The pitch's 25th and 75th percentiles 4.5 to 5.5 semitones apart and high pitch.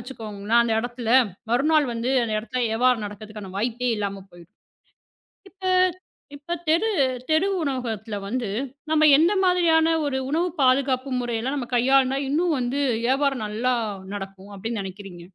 Yes: average, 4.9 semitones; very high, 250 Hz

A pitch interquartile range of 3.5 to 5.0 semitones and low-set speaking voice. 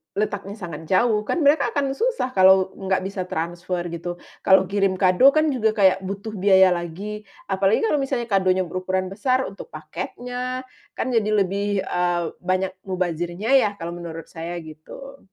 No: average, 3.8 semitones; high, 190 Hz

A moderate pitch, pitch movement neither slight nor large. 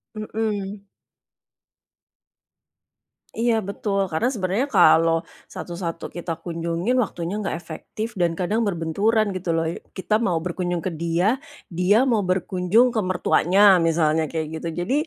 Yes: medium, 180 Hz; average, 3.9 semitones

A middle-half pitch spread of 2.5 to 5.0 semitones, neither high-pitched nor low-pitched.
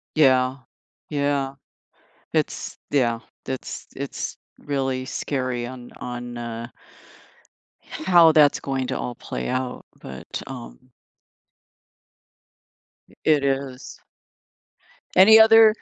No: average, 2.8 semitones; low, 130 Hz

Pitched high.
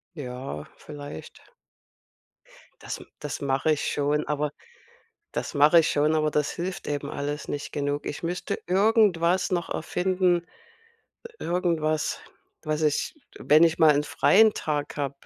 No: medium, 150 Hz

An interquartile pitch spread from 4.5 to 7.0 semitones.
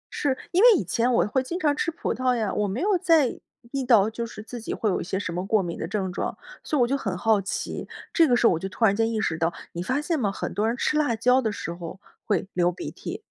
Yes: wide, 5.5 semitones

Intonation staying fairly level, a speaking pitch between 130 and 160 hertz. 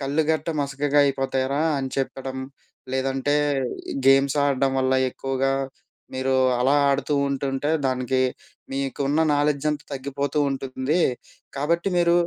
Yes: narrow, 1.4 semitones; low, 135 Hz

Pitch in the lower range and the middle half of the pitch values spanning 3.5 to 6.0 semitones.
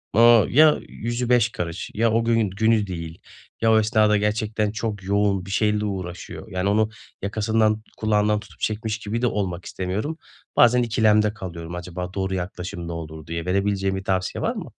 No: low, 105 Hz; average, 3.0 semitones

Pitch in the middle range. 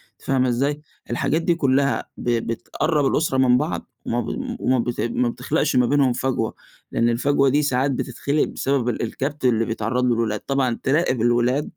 No: low, 130 Hz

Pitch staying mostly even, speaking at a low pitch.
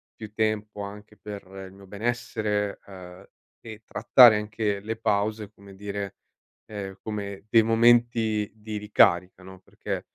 Yes: narrow, 1.6 semitones; low, 105 Hz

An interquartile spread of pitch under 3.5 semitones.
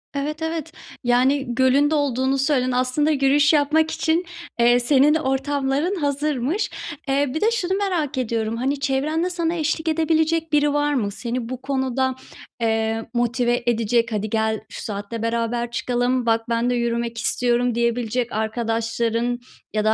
No: average, 3.9 semitones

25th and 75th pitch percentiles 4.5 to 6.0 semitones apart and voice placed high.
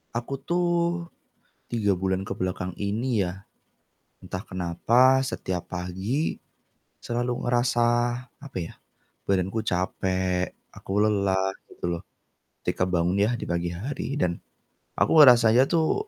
No: average, 5.1 semitones; low, 100 Hz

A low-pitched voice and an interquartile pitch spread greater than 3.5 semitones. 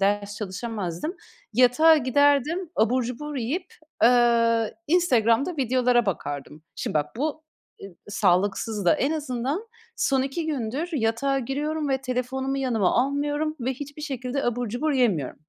No: very high, 255 Hz; average, 4.3 semitones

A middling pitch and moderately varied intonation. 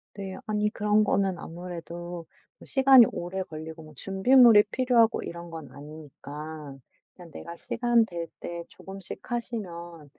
Yes: medium, 175 Hz; average, 4.4 semitones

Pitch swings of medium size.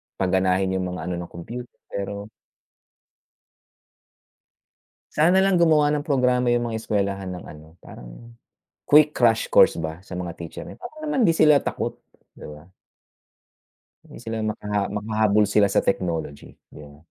No: wide, 5.7 semitones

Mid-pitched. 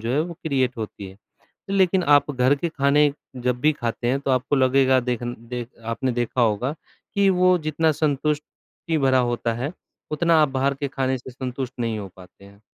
No: low, 130 Hz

